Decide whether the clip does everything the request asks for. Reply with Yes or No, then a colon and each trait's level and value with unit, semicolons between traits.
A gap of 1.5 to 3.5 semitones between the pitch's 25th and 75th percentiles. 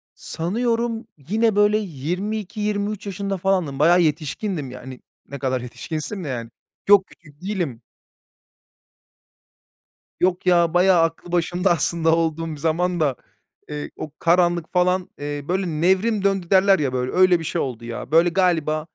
No: average, 4.0 semitones